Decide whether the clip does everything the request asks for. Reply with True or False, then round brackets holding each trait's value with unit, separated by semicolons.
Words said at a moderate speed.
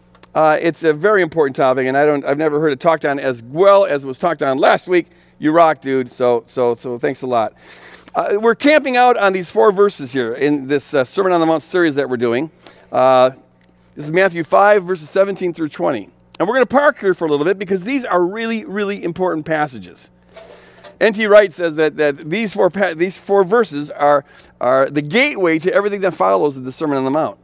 False (225 wpm)